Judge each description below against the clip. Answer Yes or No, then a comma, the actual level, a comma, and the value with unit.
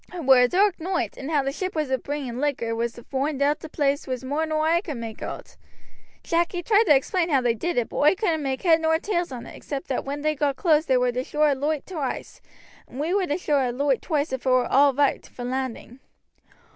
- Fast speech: Yes, fast, 260 wpm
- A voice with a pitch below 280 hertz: No, very high, 285 Hz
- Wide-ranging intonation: No, average, 3.5 semitones